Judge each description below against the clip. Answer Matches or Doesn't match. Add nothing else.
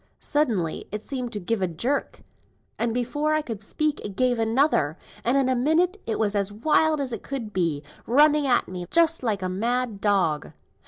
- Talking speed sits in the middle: Matches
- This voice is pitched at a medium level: Doesn't match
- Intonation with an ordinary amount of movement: Doesn't match